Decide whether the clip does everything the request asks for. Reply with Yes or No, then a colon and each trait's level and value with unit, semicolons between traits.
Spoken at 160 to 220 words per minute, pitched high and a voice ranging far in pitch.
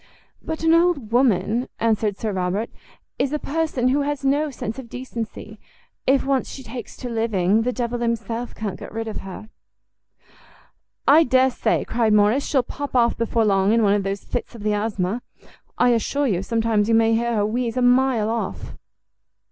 No: average, 185 wpm; high, 230 Hz; average, 3.3 semitones